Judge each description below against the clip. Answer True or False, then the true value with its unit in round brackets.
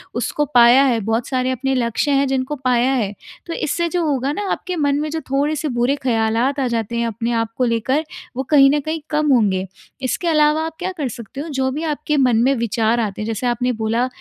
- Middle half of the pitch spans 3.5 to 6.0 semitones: True (4.1 semitones)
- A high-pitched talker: True (260 Hz)